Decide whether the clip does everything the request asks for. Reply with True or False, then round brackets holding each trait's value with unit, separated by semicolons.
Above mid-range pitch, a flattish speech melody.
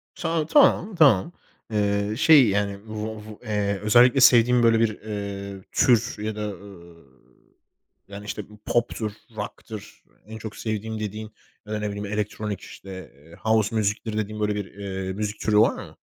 False (105 Hz; 1.6 semitones)